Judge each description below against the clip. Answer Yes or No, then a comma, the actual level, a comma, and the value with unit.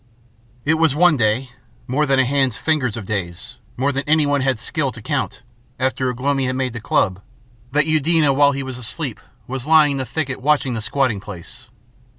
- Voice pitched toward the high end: No, low, 130 Hz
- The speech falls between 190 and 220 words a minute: Yes, average, 195 wpm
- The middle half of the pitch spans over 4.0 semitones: No, average, 3.1 semitones